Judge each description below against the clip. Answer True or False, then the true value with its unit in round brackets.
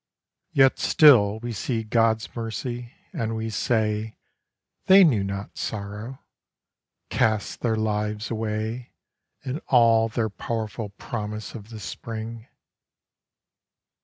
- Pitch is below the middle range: True (110 Hz)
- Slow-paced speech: True (110 wpm)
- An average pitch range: False (1.7 semitones)